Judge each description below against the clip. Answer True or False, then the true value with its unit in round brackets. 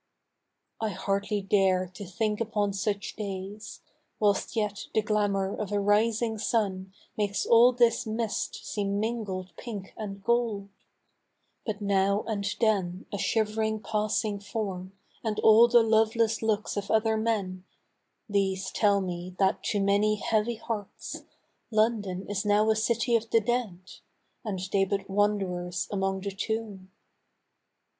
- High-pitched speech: True (210 Hz)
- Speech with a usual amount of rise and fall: False (2.0 semitones)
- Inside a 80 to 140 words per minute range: True (135 wpm)